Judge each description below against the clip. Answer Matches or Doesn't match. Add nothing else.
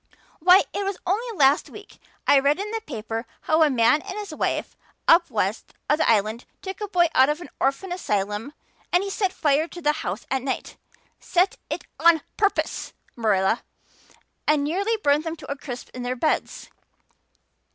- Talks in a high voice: Matches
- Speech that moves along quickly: Doesn't match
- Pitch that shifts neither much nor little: Doesn't match